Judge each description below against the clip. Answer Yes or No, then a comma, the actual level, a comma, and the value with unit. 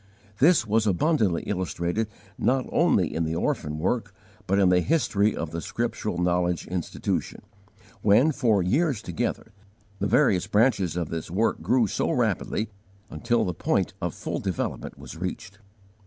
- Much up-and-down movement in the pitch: No, average, 4.5 semitones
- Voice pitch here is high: No, low, 100 Hz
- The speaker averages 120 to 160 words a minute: Yes, average, 150 wpm